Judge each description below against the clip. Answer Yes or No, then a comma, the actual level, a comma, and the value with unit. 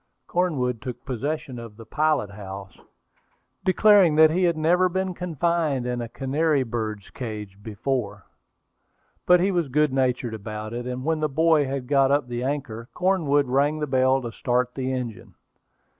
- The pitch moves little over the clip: No, average, 4.6 semitones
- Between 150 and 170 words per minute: Yes, average, 165 wpm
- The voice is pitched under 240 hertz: Yes, low, 135 Hz